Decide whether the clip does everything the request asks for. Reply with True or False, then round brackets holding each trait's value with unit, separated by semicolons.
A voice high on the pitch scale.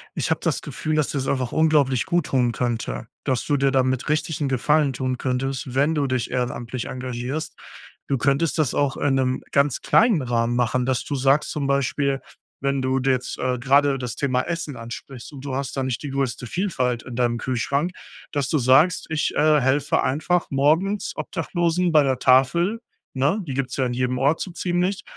False (135 Hz)